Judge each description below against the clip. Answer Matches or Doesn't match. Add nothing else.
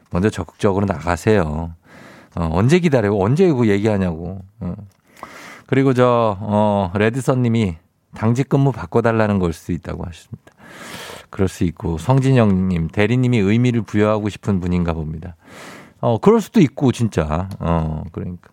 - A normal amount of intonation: Matches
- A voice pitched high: Doesn't match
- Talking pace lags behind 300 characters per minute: Doesn't match